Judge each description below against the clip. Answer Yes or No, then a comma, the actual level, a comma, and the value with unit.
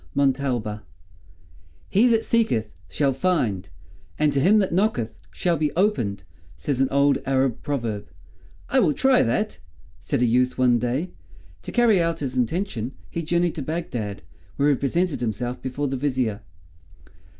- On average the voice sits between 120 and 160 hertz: Yes, medium, 140 Hz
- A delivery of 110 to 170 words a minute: Yes, average, 150 wpm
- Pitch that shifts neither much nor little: No, wide, 6.0 semitones